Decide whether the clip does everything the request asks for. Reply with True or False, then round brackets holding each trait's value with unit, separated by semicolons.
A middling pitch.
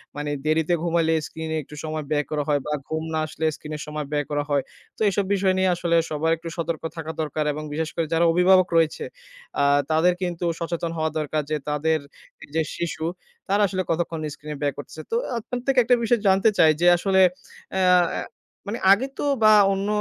True (165 Hz)